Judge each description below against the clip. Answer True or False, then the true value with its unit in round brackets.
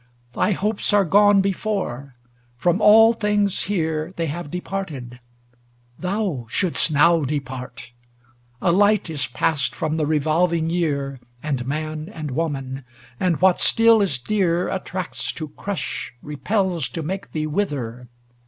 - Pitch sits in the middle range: True (165 Hz)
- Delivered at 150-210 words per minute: False (135 wpm)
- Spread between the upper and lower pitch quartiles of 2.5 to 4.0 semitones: False (5.2 semitones)